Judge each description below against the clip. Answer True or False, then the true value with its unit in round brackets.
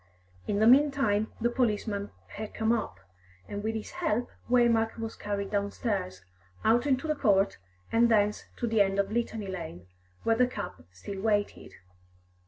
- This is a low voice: False (220 Hz)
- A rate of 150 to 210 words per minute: True (160 wpm)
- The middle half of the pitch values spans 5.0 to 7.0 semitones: False (2.8 semitones)